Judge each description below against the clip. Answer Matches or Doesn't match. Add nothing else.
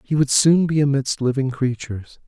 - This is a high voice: Doesn't match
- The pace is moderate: Matches